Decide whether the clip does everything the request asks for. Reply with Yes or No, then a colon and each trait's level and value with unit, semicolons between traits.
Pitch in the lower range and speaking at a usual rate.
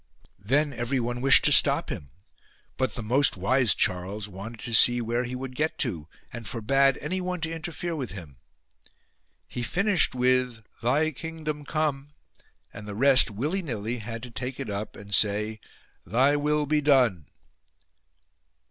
Yes: low, 125 Hz; average, 155 wpm